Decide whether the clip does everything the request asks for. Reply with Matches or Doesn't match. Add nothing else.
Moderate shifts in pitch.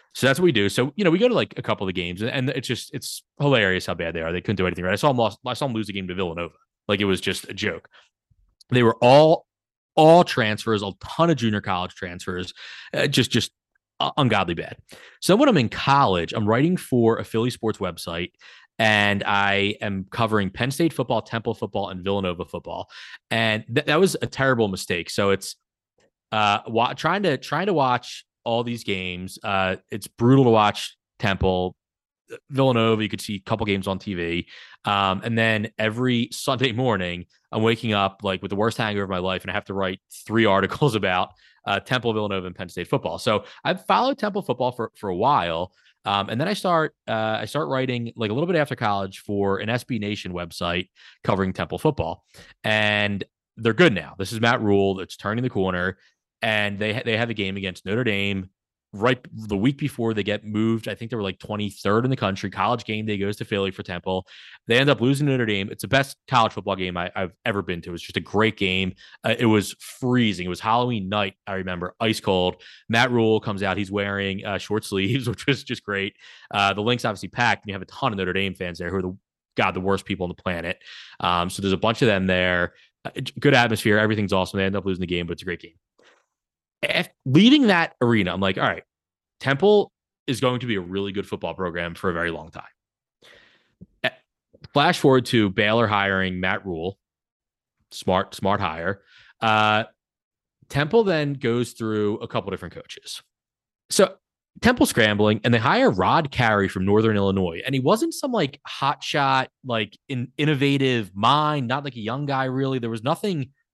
Matches